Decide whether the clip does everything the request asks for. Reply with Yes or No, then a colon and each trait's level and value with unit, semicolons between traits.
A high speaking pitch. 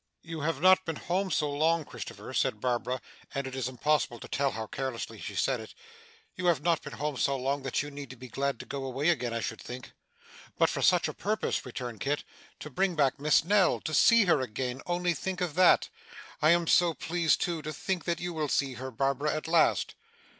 No: medium, 145 Hz